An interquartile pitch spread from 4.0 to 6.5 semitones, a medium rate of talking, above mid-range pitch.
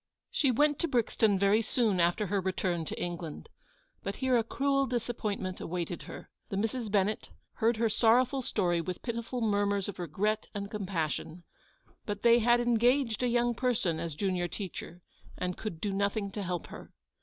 Yes: average, 4.5 semitones; average, 170 wpm; high, 205 Hz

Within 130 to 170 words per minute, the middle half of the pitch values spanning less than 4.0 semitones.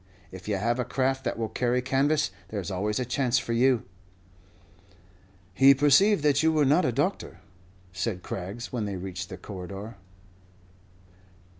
No: average, 155 wpm; average, 5.3 semitones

